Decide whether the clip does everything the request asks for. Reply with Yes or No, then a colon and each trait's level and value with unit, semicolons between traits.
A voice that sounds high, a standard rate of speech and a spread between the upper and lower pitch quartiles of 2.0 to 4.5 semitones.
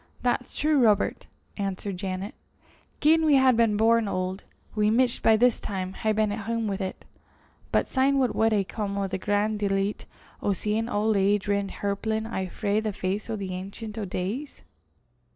Yes: high, 210 Hz; average, 185 wpm; narrow, 2.5 semitones